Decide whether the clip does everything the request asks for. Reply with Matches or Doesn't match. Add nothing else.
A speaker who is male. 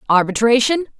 Doesn't match